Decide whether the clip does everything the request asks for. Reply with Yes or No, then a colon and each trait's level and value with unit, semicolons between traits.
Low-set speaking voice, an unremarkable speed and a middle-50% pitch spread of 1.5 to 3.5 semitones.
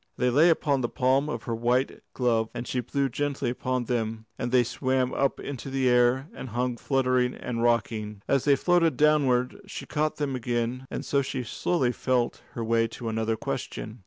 Yes: low, 125 Hz; average, 190 wpm; narrow, 2.4 semitones